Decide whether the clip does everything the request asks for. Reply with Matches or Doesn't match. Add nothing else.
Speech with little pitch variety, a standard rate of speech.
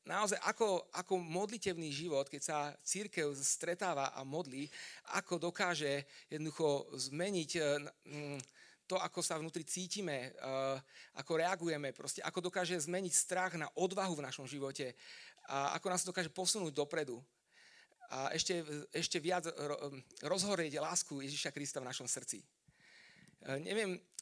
Doesn't match